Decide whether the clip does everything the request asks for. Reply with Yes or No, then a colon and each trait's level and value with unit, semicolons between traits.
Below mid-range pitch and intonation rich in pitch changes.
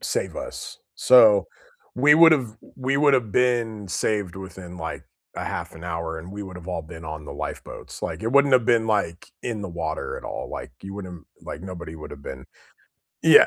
Yes: very low, 95 Hz; wide, 6.8 semitones